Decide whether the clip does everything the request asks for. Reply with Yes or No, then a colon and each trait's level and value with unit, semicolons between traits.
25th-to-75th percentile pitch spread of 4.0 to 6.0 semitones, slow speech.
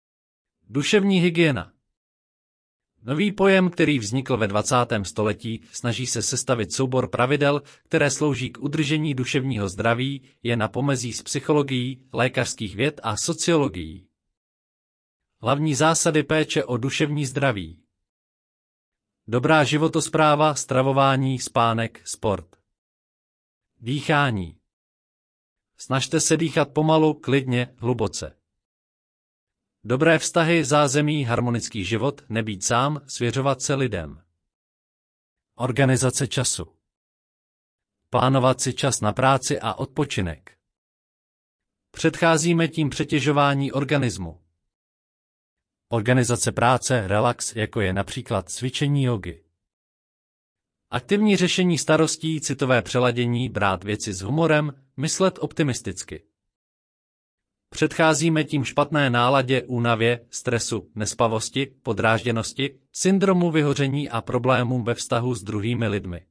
Yes: average, 5.3 semitones; slow, 95 wpm